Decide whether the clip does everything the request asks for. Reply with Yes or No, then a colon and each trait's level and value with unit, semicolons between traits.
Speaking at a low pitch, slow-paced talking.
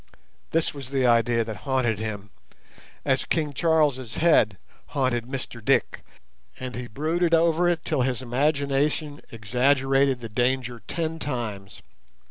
Yes: low, 130 Hz; slow, 130 wpm